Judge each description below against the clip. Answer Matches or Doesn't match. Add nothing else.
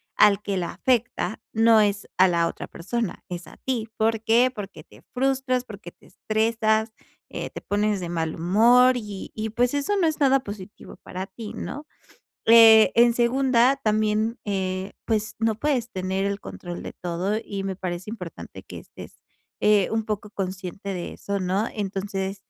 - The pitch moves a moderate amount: Matches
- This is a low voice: Doesn't match